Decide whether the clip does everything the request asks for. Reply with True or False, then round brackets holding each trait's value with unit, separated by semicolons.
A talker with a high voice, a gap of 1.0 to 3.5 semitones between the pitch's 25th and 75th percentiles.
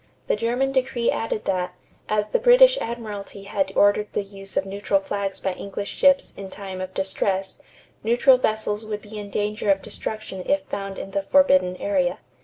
True (205 Hz; 3.1 semitones)